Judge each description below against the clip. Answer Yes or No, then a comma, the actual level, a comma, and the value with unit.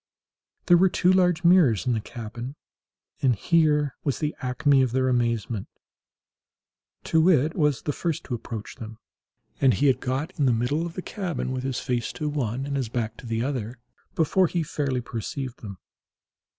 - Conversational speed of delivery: Yes, average, 180 wpm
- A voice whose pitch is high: No, low, 135 Hz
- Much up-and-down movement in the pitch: No, average, 4.5 semitones